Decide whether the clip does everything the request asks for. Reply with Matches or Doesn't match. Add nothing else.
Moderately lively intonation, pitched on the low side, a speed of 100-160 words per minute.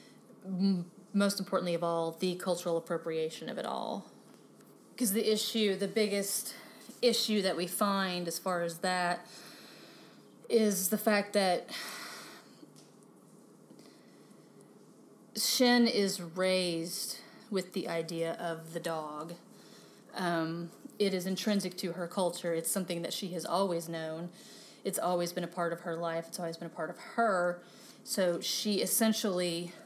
Doesn't match